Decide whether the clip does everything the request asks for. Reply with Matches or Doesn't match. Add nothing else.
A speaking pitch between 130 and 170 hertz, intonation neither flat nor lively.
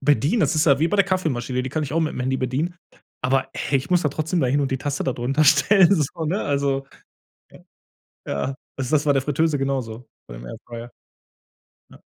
Matches